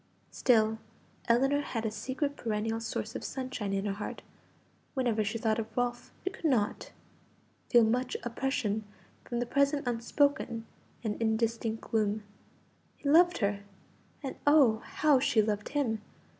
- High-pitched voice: Yes, high, 230 Hz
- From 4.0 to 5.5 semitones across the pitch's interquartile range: No, average, 3.5 semitones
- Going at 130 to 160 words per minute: Yes, average, 145 wpm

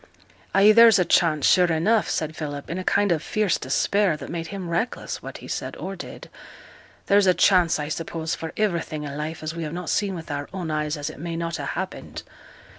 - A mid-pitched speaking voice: Yes, medium, 170 Hz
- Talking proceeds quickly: Yes, fast, 220 wpm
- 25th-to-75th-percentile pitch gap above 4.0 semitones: No, average, 3.5 semitones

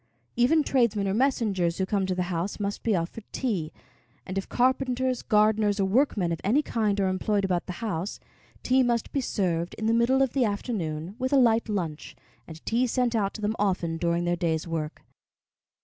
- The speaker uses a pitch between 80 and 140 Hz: No, high, 205 Hz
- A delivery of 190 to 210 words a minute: Yes, average, 195 wpm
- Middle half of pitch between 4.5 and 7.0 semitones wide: Yes, average, 5.1 semitones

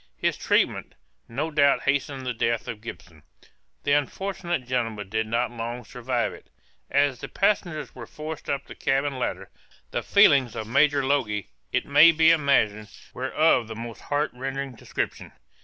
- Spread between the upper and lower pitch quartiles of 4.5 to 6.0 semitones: No, average, 4.0 semitones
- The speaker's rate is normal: Yes, average, 160 wpm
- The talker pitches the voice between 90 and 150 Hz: Yes, low, 135 Hz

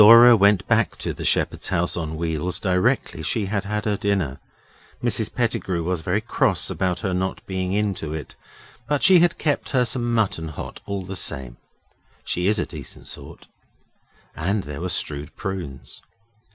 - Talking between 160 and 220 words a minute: Yes, average, 175 wpm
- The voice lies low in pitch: Yes, very low, 95 Hz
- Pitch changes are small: No, average, 4.0 semitones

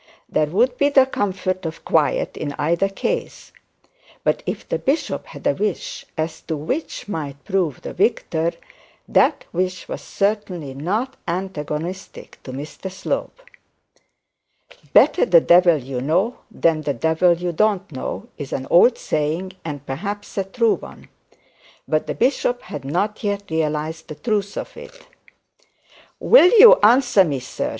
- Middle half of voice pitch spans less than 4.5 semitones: No, wide, 5.5 semitones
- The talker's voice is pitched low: No, medium, 180 Hz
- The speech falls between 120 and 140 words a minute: No, average, 150 wpm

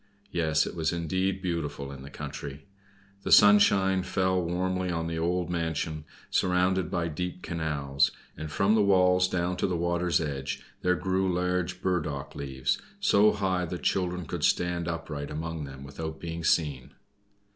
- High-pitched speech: No, very low, 85 Hz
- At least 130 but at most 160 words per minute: Yes, average, 155 wpm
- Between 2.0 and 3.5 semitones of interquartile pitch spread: Yes, average, 2.8 semitones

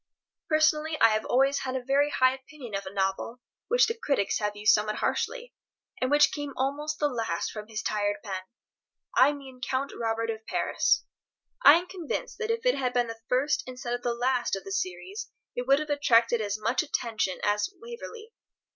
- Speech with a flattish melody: No, average, 5.1 semitones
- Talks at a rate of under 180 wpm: No, average, 195 wpm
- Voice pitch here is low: No, very high, 255 Hz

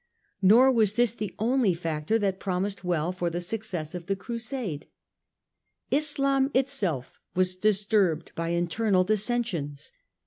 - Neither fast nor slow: No, slow, 130 wpm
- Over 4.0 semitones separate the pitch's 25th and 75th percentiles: Yes, average, 4.9 semitones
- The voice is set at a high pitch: Yes, high, 195 Hz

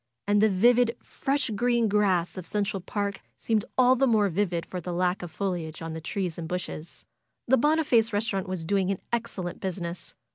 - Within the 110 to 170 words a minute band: No, average, 185 wpm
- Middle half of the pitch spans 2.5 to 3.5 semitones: No, average, 4.2 semitones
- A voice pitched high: Yes, high, 200 Hz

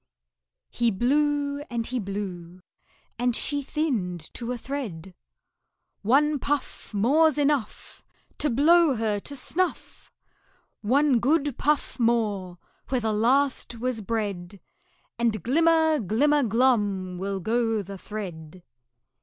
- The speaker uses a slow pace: Yes, slow, 115 wpm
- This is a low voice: No, high, 235 Hz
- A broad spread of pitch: Yes, wide, 5.9 semitones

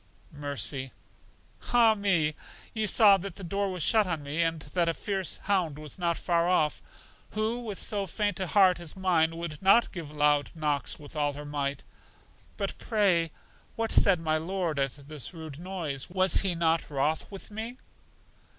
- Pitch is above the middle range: No, medium, 170 Hz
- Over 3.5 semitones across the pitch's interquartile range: Yes, average, 4.4 semitones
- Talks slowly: No, average, 175 wpm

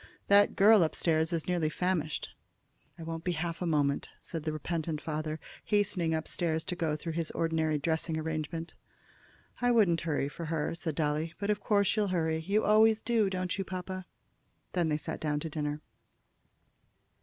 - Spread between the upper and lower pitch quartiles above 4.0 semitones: No, average, 3.0 semitones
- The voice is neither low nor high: Yes, medium, 165 Hz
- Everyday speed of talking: Yes, average, 180 wpm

